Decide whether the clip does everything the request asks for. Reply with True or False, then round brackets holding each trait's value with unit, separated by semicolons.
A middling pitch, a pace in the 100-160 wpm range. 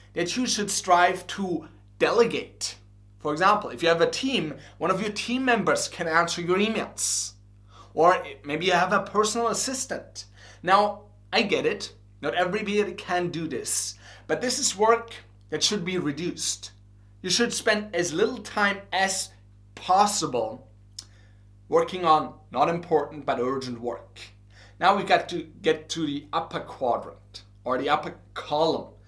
True (155 Hz; 155 wpm)